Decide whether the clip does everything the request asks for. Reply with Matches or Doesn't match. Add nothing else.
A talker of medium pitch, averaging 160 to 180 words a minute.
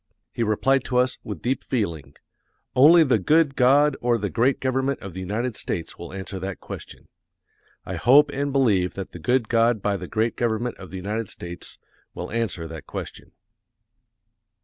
Doesn't match